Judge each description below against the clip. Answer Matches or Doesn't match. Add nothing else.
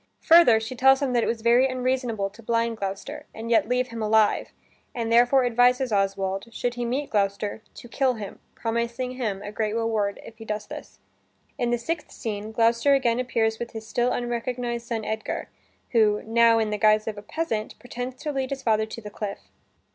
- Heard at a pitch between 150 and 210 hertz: Doesn't match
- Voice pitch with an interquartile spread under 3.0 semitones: Matches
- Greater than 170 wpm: Matches